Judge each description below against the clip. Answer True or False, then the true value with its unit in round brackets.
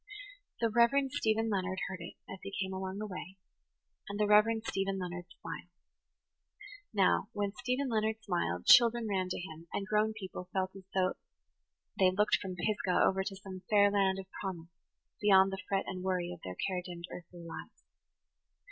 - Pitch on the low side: False (195 Hz)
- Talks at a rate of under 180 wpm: False (185 wpm)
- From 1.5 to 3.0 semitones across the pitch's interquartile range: True (2.4 semitones)